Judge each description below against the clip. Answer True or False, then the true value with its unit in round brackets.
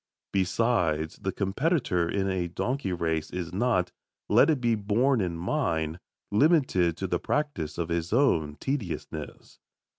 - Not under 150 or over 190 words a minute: False (140 wpm)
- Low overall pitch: True (95 Hz)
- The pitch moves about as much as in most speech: False (6.6 semitones)